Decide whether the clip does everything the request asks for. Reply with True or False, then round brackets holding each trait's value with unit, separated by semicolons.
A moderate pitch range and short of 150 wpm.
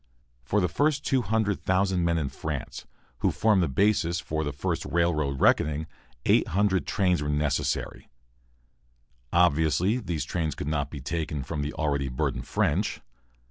True (4.5 semitones; 140 wpm)